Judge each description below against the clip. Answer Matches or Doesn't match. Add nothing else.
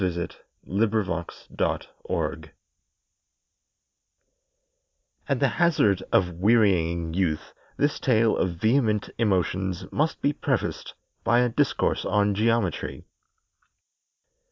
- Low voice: Matches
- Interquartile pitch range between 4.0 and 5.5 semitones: Matches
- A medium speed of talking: Doesn't match